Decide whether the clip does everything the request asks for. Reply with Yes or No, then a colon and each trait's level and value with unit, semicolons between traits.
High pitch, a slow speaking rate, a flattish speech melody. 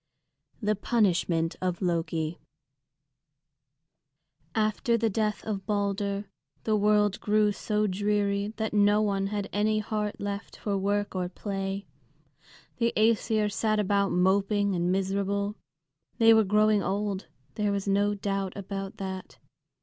Yes: high, 205 Hz; slow, 125 wpm; narrow, 1.4 semitones